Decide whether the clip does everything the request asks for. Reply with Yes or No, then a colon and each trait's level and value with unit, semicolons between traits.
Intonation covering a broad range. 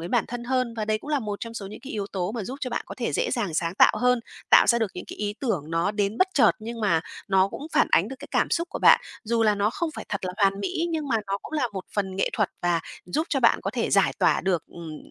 No: average, 4.1 semitones